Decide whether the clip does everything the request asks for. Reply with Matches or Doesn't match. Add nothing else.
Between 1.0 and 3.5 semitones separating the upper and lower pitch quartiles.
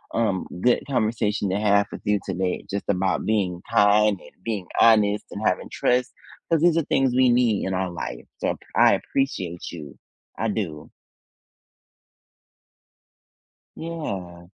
Doesn't match